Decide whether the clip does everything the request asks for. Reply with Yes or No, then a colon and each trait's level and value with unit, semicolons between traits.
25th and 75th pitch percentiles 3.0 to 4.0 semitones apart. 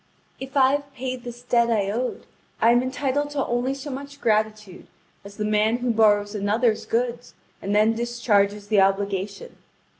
Yes: average, 3.6 semitones